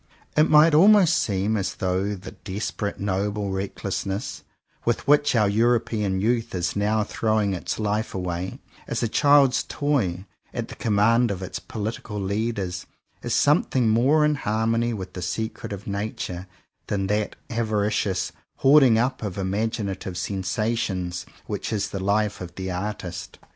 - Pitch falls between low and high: No, low, 105 Hz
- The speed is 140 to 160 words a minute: Yes, average, 150 wpm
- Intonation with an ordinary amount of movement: Yes, average, 3.3 semitones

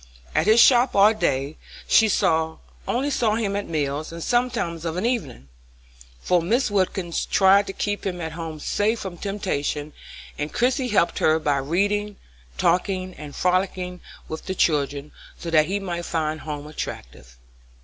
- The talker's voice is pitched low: No, medium, 180 Hz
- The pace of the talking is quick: No, average, 160 wpm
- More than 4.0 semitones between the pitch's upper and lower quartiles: Yes, average, 4.8 semitones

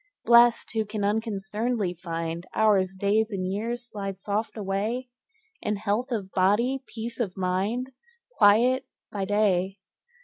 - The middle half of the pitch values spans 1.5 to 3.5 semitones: Yes, average, 3.2 semitones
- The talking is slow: Yes, slow, 130 wpm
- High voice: Yes, high, 210 Hz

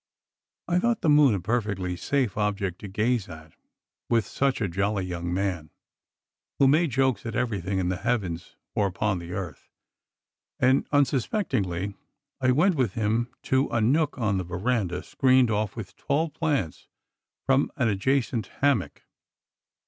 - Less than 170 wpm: Yes, average, 150 wpm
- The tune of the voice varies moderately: No, wide, 5.8 semitones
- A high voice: No, low, 110 Hz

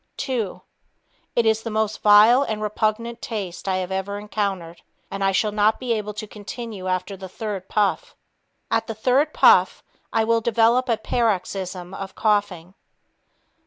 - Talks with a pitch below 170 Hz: No, high, 210 Hz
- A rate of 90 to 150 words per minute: No, average, 160 wpm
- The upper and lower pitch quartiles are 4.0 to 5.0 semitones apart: No, narrow, 2.6 semitones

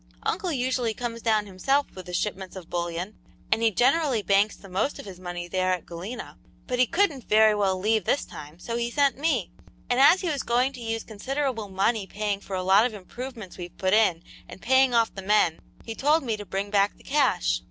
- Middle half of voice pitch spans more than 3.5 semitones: Yes, average, 5.0 semitones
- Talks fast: Yes, fast, 220 wpm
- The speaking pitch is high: Yes, high, 215 Hz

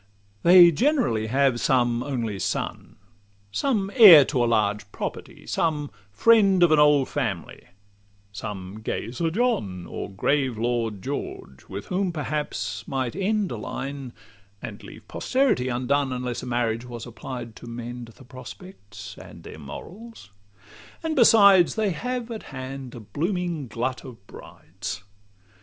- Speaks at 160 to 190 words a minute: No, average, 140 wpm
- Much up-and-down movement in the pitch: Yes, wide, 7.5 semitones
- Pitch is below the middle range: Yes, low, 130 Hz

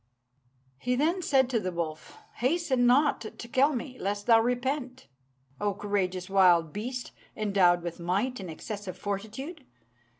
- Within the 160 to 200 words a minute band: No, average, 145 wpm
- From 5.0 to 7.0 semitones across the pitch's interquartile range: Yes, wide, 5.4 semitones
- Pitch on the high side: Yes, high, 220 Hz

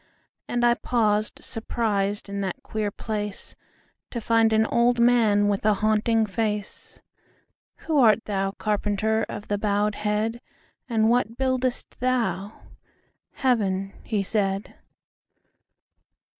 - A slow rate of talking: Yes, slow, 90 wpm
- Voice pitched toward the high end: Yes, high, 215 Hz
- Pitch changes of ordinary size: No, narrow, 2.3 semitones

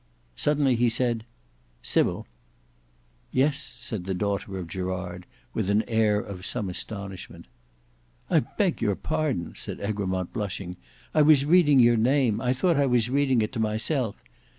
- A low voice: Yes, low, 110 Hz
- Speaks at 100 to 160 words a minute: Yes, average, 150 wpm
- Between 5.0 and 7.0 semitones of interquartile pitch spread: Yes, average, 5.3 semitones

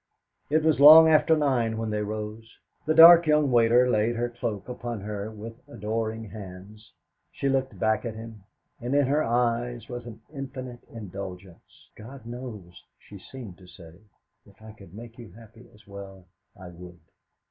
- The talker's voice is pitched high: No, low, 115 Hz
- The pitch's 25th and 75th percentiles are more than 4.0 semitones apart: No, average, 3.2 semitones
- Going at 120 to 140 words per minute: No, average, 170 wpm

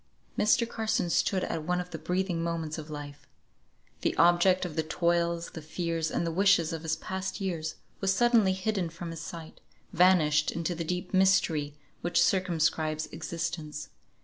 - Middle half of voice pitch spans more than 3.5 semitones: No, average, 2.8 semitones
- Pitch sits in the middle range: Yes, medium, 170 Hz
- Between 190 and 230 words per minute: No, average, 165 wpm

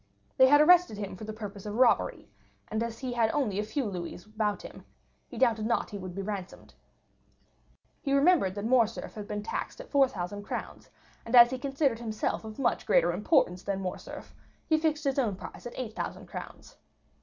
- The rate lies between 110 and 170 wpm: No, average, 190 wpm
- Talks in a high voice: Yes, high, 220 Hz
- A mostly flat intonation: No, average, 4.5 semitones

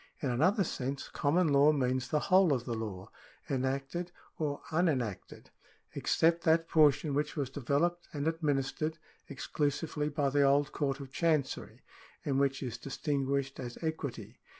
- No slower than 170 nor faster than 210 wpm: No, average, 155 wpm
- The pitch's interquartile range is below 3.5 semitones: Yes, average, 2.9 semitones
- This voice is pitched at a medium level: Yes, medium, 145 Hz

